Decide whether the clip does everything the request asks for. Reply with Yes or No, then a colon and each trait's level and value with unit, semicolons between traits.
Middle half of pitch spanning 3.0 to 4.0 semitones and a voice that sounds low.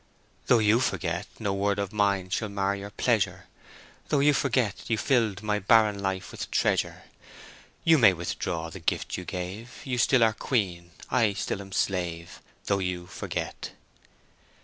Yes: average, 3.4 semitones; low, 100 Hz